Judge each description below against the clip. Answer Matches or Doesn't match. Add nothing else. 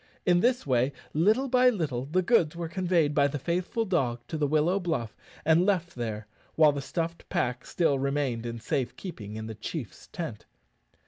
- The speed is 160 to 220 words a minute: Matches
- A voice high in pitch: Doesn't match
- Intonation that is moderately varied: Doesn't match